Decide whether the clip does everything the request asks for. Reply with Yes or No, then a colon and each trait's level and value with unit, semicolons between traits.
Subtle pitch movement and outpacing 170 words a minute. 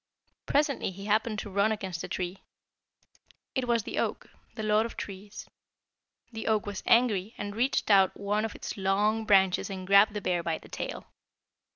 Yes: narrow, 2.3 semitones; average, 180 wpm